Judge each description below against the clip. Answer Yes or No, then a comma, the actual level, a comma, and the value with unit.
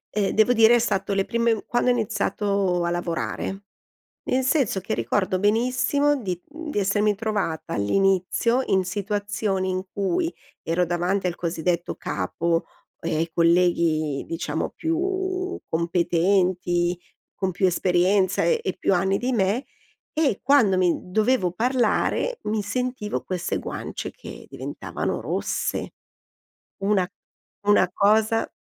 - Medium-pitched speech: No, high, 195 Hz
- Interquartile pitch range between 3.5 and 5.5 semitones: Yes, average, 4.5 semitones